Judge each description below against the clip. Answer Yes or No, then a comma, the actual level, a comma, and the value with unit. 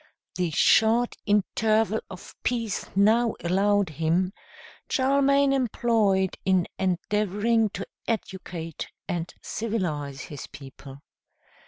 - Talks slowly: Yes, slow, 95 wpm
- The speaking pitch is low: No, high, 200 Hz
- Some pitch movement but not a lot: Yes, average, 4.4 semitones